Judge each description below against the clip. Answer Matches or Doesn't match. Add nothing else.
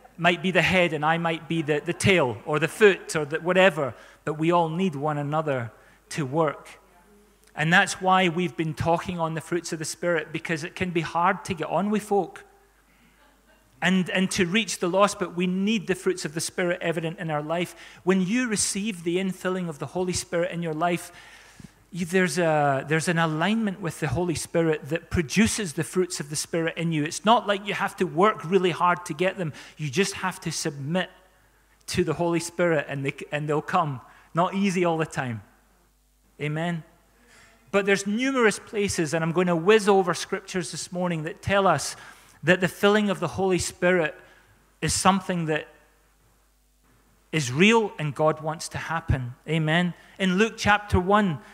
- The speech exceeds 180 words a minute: Matches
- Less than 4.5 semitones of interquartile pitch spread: Matches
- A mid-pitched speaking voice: Matches